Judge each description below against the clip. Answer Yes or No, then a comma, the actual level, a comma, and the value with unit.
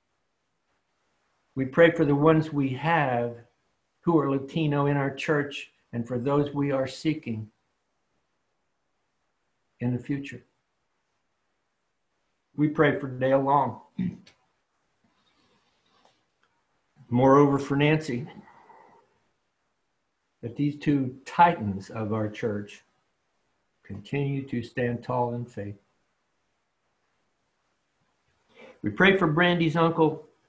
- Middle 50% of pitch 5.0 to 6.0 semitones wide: No, average, 4.2 semitones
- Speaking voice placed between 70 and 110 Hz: No, medium, 140 Hz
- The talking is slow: Yes, slow, 95 wpm